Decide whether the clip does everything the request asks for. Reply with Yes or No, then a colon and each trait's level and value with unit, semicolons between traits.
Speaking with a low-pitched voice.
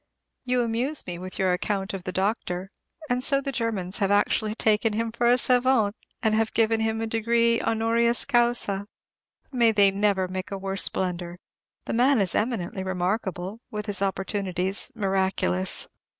No: high, 210 Hz